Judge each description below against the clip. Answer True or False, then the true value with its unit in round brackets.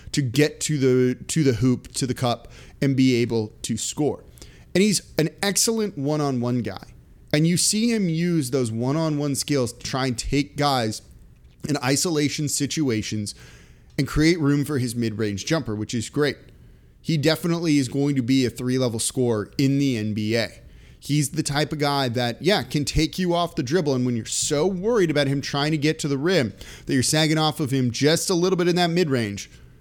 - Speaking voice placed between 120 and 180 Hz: True (140 Hz)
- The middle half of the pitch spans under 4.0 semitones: False (4.3 semitones)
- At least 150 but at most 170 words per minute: False (195 wpm)